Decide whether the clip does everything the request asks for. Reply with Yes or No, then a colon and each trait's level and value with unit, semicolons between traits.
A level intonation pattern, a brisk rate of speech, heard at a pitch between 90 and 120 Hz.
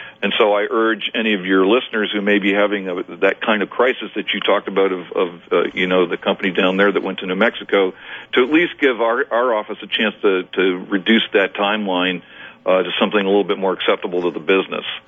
Yes: narrow, 1.9 semitones; fast, 235 wpm; low, 100 Hz